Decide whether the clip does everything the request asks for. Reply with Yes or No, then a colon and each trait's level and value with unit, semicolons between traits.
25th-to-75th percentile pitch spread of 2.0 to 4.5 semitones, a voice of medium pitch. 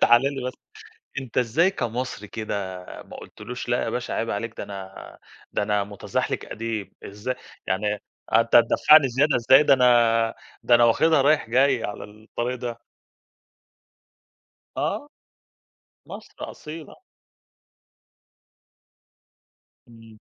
No: average, 3.1 semitones; low, 115 Hz